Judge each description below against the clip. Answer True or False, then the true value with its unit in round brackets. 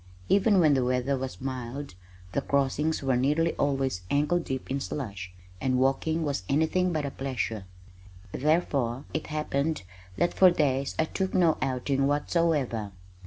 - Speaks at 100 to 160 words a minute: True (150 wpm)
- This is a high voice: False (140 Hz)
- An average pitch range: True (3.4 semitones)